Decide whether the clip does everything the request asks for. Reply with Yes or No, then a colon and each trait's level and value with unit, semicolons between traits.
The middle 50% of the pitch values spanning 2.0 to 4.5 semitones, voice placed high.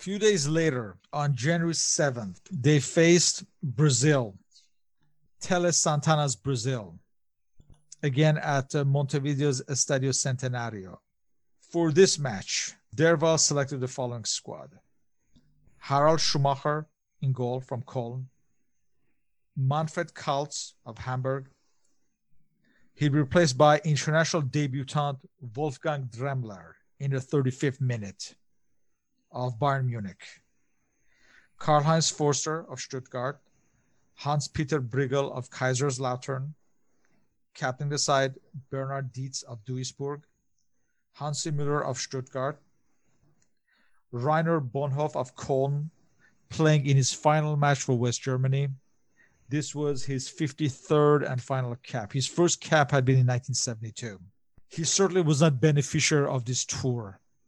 No: average, 2.9 semitones; medium, 140 Hz